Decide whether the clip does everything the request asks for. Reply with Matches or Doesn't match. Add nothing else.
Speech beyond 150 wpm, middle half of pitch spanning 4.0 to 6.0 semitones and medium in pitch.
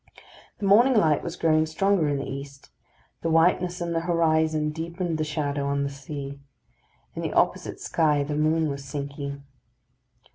Doesn't match